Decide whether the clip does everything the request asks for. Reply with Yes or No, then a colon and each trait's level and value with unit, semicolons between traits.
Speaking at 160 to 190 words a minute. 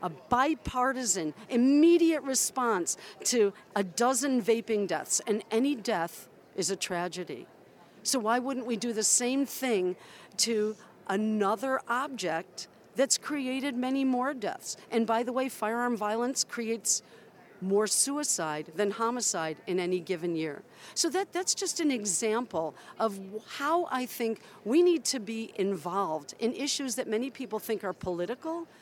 No: average, 145 wpm